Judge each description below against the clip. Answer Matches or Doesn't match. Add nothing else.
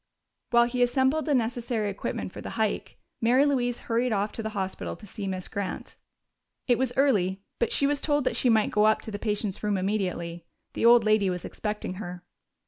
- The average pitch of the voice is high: Matches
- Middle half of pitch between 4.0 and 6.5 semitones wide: Doesn't match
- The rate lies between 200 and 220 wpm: Matches